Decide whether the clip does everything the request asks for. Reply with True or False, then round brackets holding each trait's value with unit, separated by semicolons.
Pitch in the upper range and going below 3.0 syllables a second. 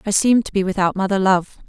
False (195 Hz; 6.8 syllables/s)